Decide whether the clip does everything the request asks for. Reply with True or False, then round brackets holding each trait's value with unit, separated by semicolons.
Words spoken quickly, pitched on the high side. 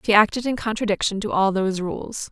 True (210 wpm; 210 Hz)